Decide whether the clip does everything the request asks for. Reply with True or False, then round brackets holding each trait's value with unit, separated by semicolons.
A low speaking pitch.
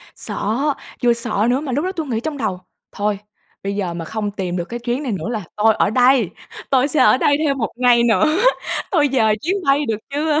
False (240 Hz)